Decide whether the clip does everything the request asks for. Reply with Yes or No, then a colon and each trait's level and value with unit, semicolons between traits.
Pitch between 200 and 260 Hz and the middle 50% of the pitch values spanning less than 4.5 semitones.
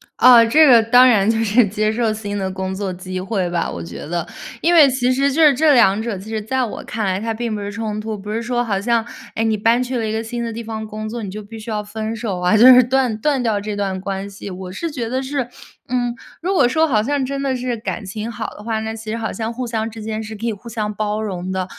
Yes: high, 220 Hz; average, 2.8 semitones